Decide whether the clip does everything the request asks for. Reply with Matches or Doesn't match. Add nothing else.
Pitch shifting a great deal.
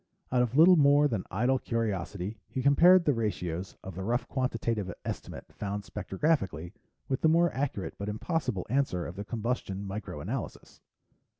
Matches